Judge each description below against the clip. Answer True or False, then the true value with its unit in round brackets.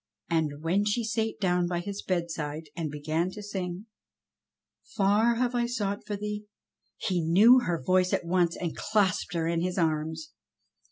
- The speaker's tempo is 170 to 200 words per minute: True (175 wpm)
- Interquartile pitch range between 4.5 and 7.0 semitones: False (4.0 semitones)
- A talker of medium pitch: True (180 Hz)